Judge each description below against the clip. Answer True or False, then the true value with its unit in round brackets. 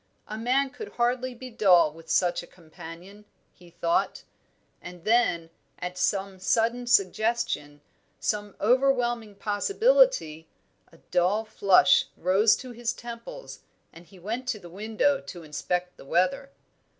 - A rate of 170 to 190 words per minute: False (135 wpm)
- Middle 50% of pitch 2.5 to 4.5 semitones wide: False (5.4 semitones)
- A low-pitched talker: False (210 Hz)